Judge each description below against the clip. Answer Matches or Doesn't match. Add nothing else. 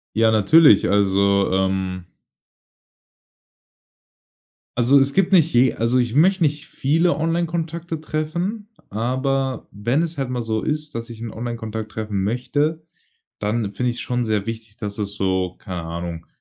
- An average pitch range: Doesn't match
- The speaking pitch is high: Doesn't match